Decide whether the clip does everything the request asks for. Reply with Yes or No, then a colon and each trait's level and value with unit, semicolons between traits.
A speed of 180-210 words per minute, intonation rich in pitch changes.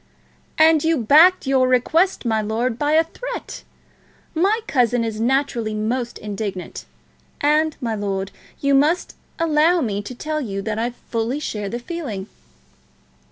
No: average, 145 wpm; wide, 6.1 semitones